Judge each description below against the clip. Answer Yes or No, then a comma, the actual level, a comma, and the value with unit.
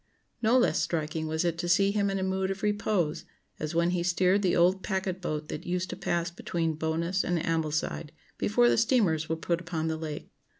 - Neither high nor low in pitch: Yes, medium, 175 Hz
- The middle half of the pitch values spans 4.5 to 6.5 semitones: No, average, 2.9 semitones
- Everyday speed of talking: No, fast, 210 wpm